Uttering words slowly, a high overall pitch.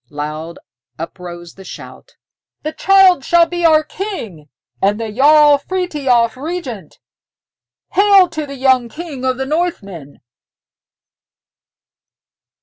Yes: slow, 110 wpm; very high, 270 Hz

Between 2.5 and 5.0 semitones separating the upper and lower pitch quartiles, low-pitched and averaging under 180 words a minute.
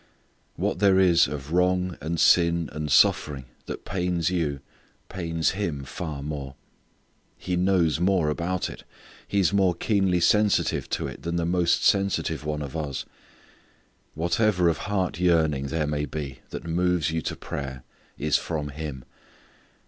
Yes: average, 3.3 semitones; very low, 85 Hz; average, 150 wpm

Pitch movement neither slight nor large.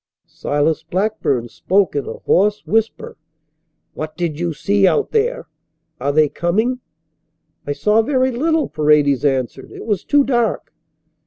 No: wide, 8.0 semitones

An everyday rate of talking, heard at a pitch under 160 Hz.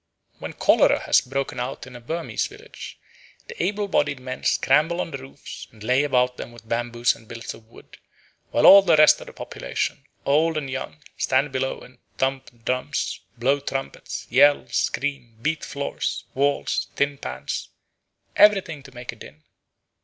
Yes: average, 170 wpm; low, 135 Hz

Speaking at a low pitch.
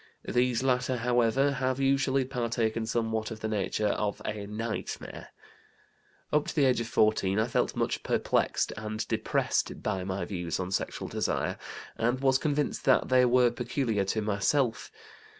Yes: low, 115 Hz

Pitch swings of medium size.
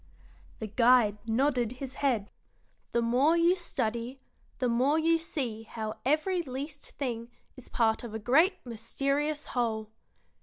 Yes: average, 4.3 semitones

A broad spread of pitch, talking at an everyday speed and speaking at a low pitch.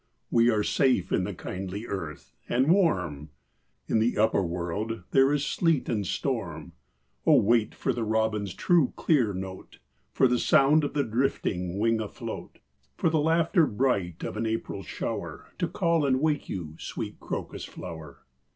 Yes: wide, 6.6 semitones; average, 160 wpm; low, 115 Hz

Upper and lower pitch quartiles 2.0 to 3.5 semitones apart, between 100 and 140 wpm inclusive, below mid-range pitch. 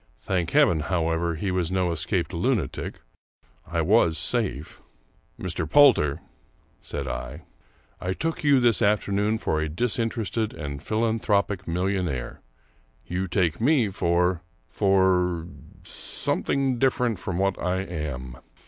No: average, 4.8 semitones; slow, 135 wpm; very low, 95 Hz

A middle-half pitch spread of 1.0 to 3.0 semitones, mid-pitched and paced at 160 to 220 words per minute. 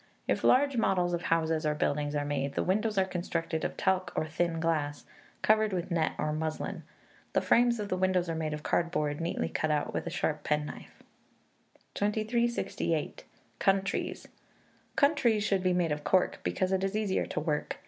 No: average, 4.3 semitones; medium, 175 Hz; average, 180 wpm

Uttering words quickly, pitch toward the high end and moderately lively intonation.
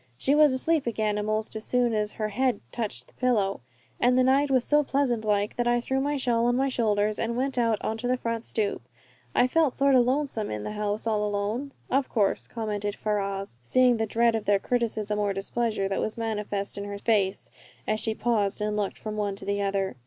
Yes: fast, 220 wpm; high, 220 Hz; average, 3.3 semitones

